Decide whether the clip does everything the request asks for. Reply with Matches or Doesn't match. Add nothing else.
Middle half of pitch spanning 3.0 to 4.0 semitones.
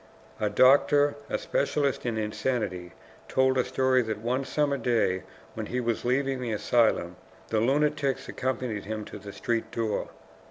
Matches